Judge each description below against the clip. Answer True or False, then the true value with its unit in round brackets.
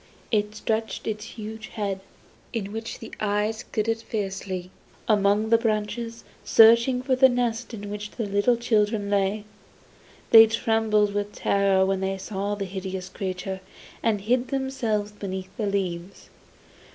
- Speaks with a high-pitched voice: True (210 Hz)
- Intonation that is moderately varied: False (2.3 semitones)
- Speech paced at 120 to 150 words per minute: True (140 wpm)